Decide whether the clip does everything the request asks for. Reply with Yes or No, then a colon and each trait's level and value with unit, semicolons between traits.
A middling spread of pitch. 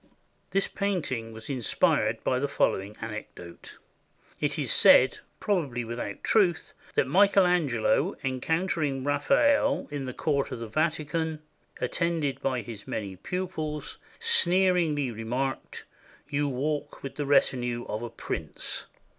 No: wide, 5.8 semitones